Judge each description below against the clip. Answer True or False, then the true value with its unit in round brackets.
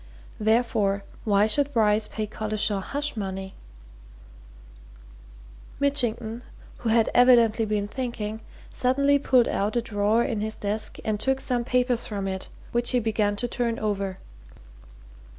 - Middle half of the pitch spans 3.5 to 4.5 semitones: False (2.8 semitones)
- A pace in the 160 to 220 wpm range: False (135 wpm)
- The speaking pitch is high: True (220 Hz)